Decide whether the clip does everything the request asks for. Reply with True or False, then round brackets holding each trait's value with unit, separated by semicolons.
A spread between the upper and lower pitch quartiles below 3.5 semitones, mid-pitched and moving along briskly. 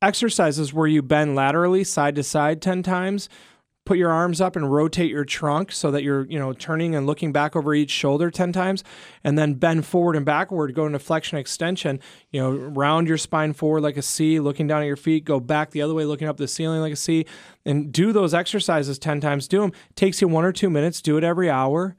True (2.9 semitones; 155 Hz; 235 wpm)